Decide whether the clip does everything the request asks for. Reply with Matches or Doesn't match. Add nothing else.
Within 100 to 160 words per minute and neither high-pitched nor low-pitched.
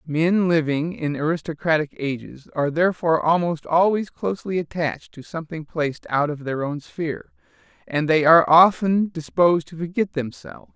Matches